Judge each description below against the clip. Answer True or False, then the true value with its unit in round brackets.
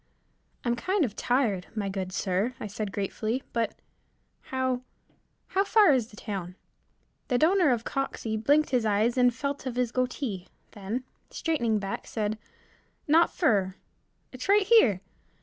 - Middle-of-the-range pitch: False (240 Hz)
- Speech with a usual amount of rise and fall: True (4.7 semitones)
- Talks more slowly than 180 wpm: True (150 wpm)